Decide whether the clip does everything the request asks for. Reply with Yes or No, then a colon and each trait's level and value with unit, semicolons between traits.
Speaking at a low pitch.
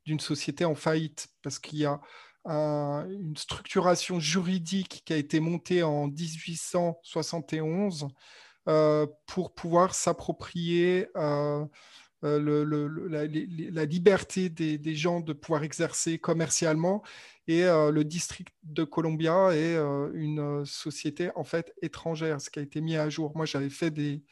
No: medium, 160 Hz